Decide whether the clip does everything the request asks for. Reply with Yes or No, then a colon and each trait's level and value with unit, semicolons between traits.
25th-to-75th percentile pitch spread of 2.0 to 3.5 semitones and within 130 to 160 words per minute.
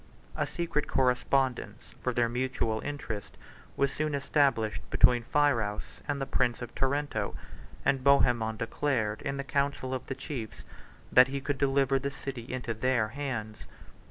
Yes: average, 3.2 semitones; average, 150 wpm